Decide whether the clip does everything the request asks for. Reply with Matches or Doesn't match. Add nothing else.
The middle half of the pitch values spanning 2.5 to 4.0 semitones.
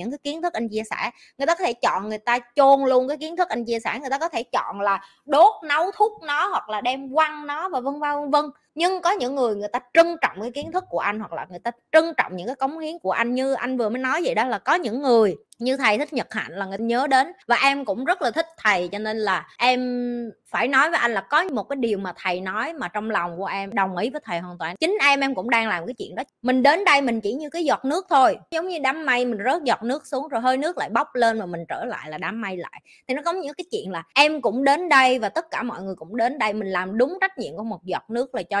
Doesn't match